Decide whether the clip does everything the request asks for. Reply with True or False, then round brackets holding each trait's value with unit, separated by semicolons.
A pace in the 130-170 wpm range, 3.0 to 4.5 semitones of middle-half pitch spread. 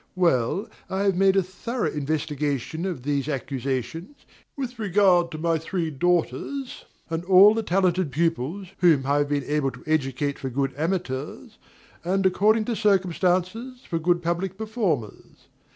False (150 wpm; 5.0 semitones)